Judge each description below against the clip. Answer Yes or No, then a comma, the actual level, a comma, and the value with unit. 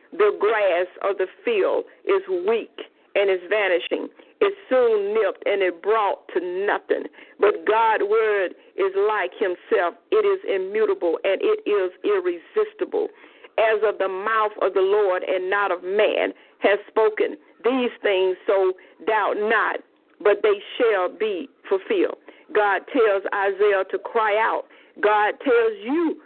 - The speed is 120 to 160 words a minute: Yes, average, 145 wpm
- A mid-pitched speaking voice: No, very high, 380 Hz